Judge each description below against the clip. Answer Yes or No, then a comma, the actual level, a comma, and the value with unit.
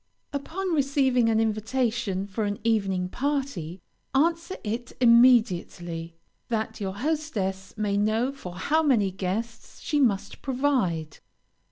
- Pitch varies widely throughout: Yes, wide, 5.7 semitones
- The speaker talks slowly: Yes, slow, 120 wpm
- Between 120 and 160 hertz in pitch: No, high, 225 Hz